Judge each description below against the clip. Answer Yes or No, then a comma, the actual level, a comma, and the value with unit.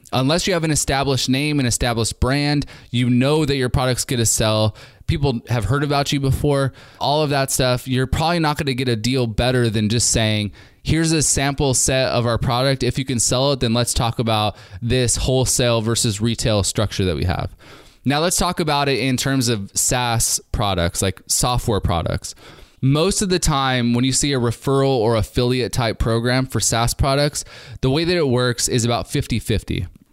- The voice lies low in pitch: Yes, low, 125 Hz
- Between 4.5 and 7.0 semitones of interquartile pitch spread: No, average, 3.1 semitones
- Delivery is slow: No, average, 200 wpm